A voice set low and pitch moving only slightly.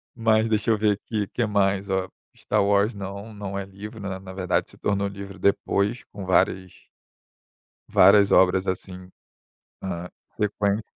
Yes: low, 100 Hz; narrow, 1.6 semitones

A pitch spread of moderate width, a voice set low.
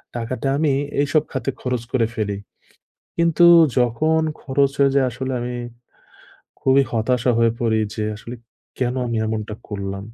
Yes: average, 3.4 semitones; low, 125 Hz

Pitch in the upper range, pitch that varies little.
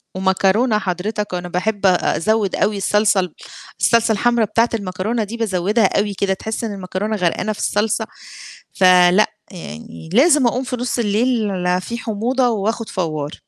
No: high, 210 Hz; average, 3.4 semitones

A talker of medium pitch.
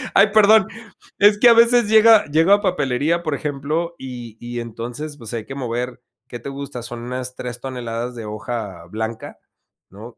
No: low, 130 Hz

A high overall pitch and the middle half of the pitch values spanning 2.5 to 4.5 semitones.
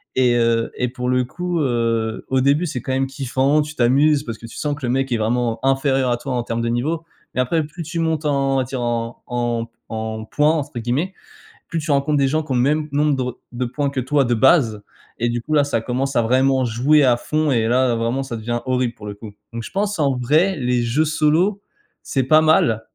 No: low, 130 Hz; average, 3.7 semitones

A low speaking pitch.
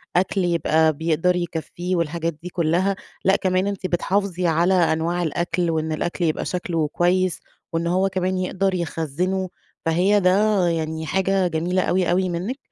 No: medium, 175 Hz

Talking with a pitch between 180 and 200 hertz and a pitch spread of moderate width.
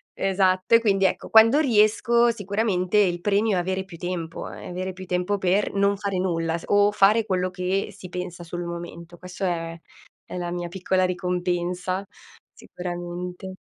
No: medium, 185 Hz; narrow, 2.1 semitones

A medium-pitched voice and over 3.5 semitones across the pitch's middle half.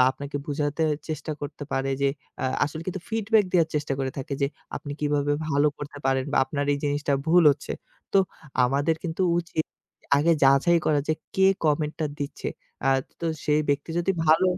No: medium, 150 Hz; narrow, 2.4 semitones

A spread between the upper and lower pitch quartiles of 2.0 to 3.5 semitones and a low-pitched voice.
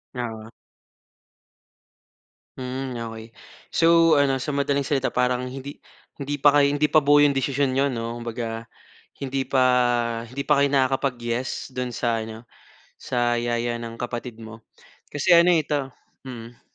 Yes: average, 3.0 semitones; low, 130 Hz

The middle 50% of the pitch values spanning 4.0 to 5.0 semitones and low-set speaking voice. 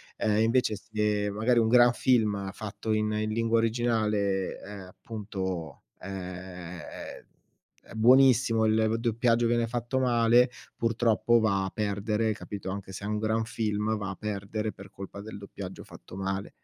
No: narrow, 2.5 semitones; low, 110 Hz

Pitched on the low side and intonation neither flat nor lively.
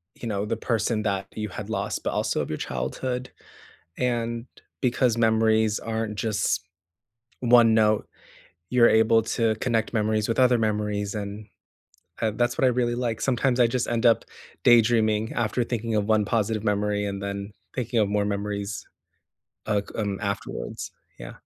No: low, 110 Hz; narrow, 2.2 semitones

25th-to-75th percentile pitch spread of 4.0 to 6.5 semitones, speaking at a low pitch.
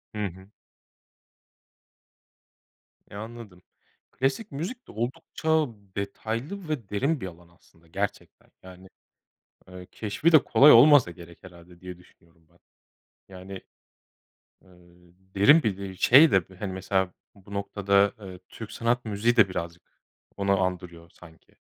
Yes: average, 4.6 semitones; low, 100 Hz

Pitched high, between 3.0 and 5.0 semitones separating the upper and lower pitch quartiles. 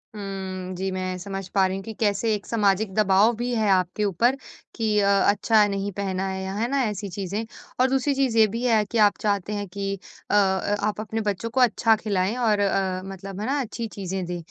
No: high, 205 Hz; narrow, 2.5 semitones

